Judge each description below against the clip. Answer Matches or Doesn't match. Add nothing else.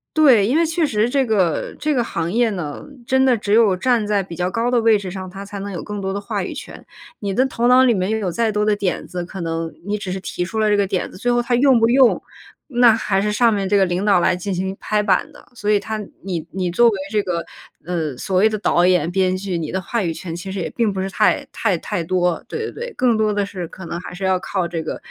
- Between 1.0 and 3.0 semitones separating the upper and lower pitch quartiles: Doesn't match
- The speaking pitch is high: Matches